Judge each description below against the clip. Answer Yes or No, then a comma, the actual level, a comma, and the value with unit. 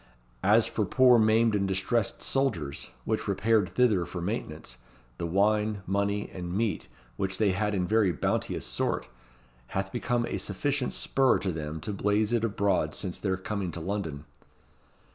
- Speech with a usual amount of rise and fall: Yes, average, 3.0 semitones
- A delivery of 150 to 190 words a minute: Yes, average, 160 wpm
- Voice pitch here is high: No, low, 100 Hz